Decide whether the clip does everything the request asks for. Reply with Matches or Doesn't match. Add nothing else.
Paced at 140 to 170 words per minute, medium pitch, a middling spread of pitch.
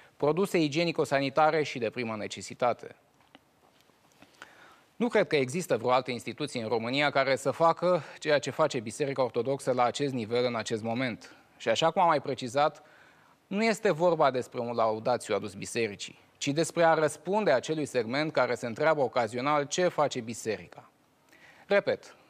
Matches